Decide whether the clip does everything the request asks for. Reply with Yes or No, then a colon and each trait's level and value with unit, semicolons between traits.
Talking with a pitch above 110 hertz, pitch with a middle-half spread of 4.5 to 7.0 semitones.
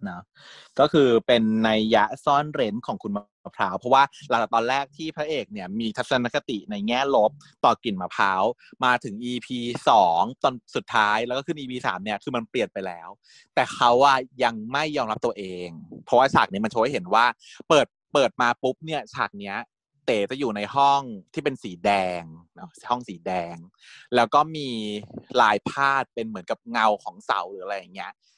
Yes: low, 120 Hz; average, 4.9 semitones